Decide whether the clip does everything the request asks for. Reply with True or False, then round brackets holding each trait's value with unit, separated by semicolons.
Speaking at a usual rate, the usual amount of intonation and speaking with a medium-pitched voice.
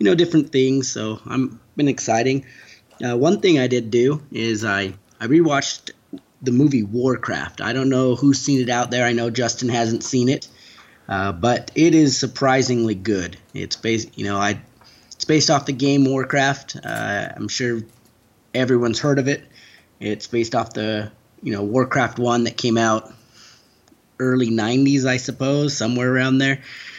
False (170 wpm; 3.0 semitones; 120 Hz)